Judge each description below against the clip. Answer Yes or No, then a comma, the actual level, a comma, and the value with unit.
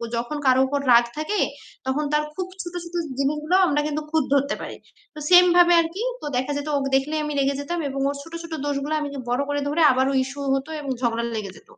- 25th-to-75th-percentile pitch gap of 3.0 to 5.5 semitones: No, narrow, 2.6 semitones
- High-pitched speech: Yes, very high, 290 Hz